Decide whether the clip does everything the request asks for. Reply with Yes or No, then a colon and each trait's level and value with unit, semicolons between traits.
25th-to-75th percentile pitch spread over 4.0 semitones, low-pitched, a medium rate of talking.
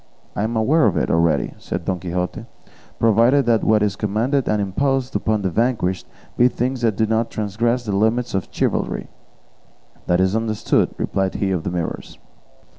No: average, 3.7 semitones; low, 110 Hz; average, 170 wpm